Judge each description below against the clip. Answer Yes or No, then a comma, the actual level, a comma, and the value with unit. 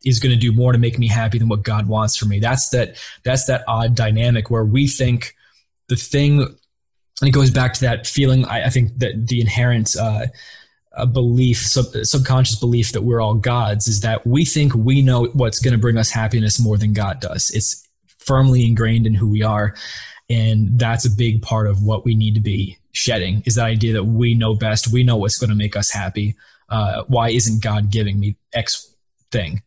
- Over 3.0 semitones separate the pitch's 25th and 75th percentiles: No, narrow, 2.4 semitones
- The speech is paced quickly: Yes, fast, 215 wpm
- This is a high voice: No, low, 115 Hz